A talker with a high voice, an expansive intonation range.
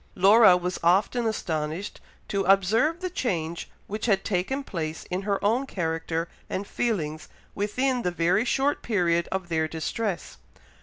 No: high, 195 Hz; average, 4.9 semitones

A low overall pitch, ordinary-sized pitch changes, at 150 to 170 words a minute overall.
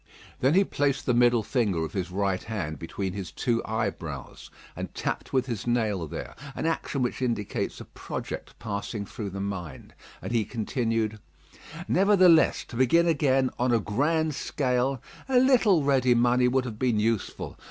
Yes: low, 120 Hz; average, 4.7 semitones; average, 165 wpm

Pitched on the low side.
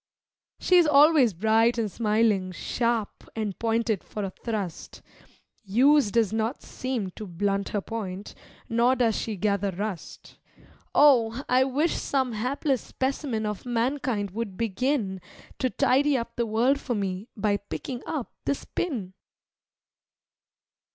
No: high, 230 Hz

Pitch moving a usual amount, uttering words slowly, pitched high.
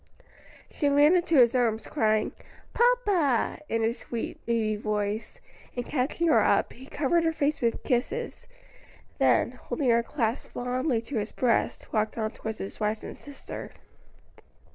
No: average, 4.7 semitones; average, 150 wpm; high, 245 Hz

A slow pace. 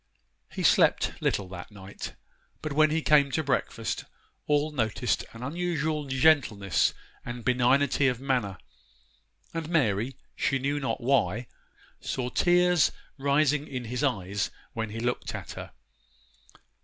Yes: slow, 130 wpm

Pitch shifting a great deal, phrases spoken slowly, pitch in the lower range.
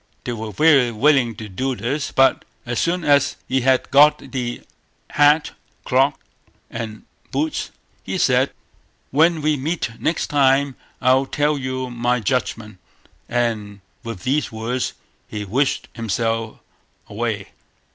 No: average, 3.8 semitones; slow, 130 wpm; low, 130 Hz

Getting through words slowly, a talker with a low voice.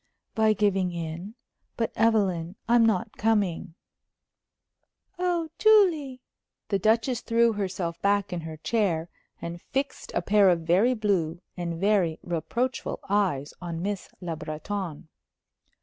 No: slow, 125 wpm; high, 200 Hz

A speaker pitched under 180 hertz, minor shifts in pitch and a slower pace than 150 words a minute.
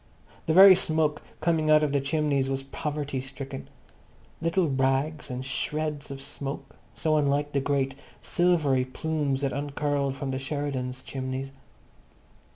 Yes: medium, 140 Hz; narrow, 2.2 semitones; average, 140 wpm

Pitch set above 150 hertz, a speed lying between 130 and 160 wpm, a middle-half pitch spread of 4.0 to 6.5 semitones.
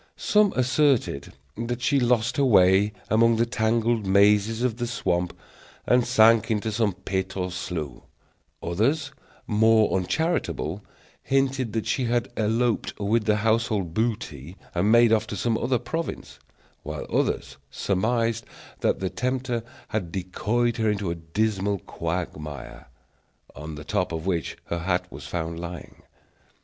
No: low, 110 Hz; average, 140 wpm; average, 4.6 semitones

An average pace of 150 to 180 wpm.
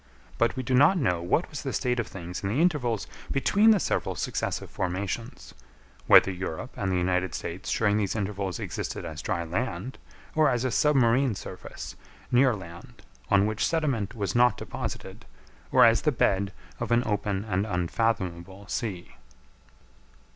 Yes: average, 160 wpm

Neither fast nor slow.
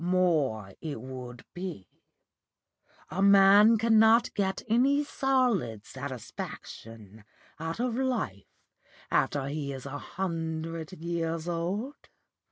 No: slow, 100 wpm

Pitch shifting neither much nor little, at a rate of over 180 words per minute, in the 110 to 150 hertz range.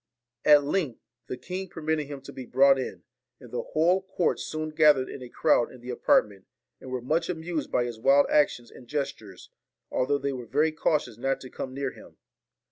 Yes: average, 3.5 semitones; average, 200 wpm; medium, 140 Hz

